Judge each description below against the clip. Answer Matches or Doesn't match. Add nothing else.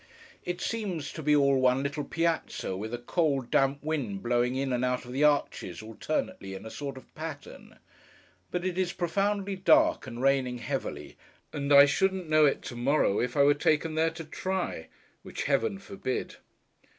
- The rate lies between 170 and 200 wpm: Matches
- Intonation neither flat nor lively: Matches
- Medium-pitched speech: Matches